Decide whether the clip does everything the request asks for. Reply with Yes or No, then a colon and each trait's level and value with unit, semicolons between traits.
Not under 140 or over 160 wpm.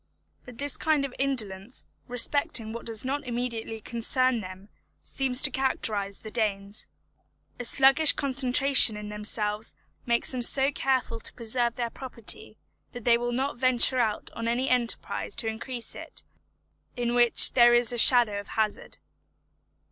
Yes: average, 150 wpm